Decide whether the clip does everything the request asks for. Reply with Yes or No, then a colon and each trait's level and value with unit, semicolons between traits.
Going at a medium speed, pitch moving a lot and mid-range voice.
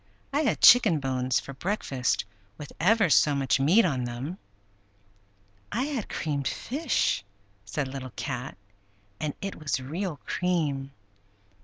No: slow, 130 wpm; wide, 6.5 semitones; medium, 145 Hz